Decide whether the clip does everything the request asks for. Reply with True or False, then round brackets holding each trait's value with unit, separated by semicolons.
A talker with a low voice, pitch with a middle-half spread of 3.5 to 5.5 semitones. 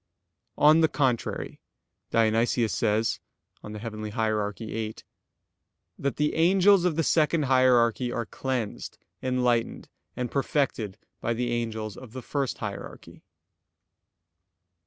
True (120 Hz; 3.9 semitones)